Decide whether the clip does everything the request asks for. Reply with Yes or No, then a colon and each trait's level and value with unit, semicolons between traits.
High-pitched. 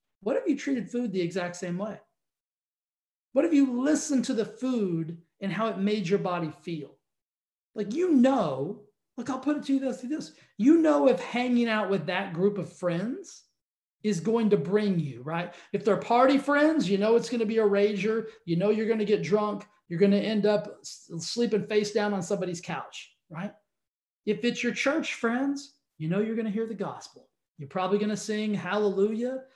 Yes: high, 210 Hz